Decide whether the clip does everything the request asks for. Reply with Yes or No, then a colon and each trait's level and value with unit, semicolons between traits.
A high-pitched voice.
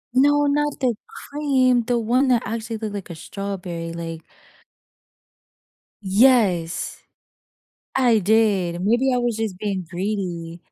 Yes: high, 215 Hz